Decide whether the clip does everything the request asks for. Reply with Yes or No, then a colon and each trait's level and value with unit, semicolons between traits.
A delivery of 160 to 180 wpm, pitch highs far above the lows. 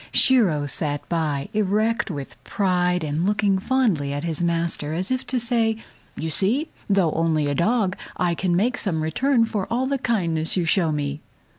Yes: average, 175 wpm; wide, 5.8 semitones